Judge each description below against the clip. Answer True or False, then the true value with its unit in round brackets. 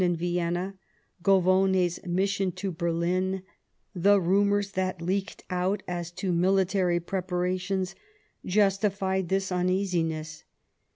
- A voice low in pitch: False (185 Hz)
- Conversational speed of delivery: False (100 wpm)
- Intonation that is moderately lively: False (1.7 semitones)